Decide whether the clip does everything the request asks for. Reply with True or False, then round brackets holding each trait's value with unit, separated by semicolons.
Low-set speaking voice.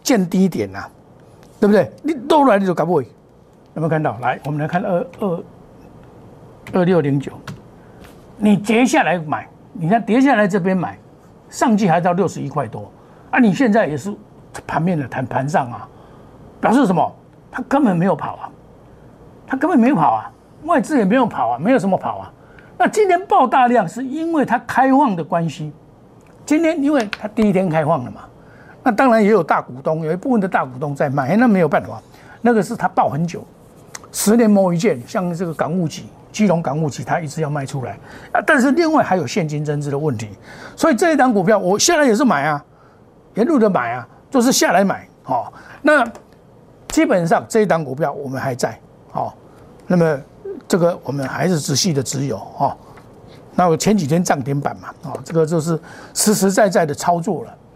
False (185 Hz)